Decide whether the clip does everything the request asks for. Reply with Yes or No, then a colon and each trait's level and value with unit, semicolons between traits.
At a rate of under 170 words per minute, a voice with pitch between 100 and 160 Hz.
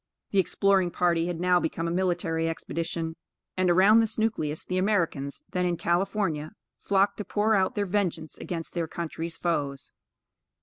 No: average, 160 wpm; medium, 175 Hz